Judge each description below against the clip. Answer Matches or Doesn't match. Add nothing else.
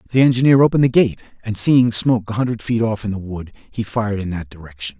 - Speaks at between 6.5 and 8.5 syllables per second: Matches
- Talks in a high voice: Doesn't match